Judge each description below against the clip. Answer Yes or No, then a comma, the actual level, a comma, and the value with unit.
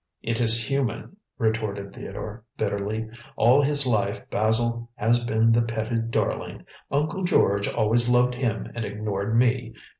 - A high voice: No, low, 115 Hz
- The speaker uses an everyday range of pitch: No, narrow, 2.1 semitones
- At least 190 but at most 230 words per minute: No, average, 140 wpm